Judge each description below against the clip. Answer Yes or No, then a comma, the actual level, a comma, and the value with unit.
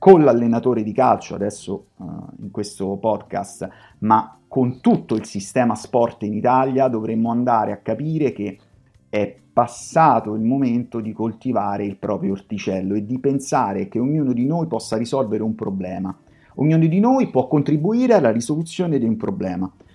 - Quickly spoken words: No, average, 155 wpm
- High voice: No, low, 115 Hz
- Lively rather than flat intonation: No, average, 4.4 semitones